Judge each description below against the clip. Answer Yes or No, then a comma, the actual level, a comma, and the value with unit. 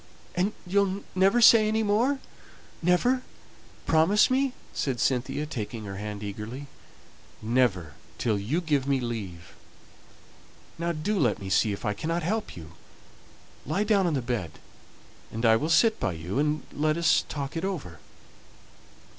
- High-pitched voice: No, medium, 150 Hz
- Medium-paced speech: Yes, average, 145 wpm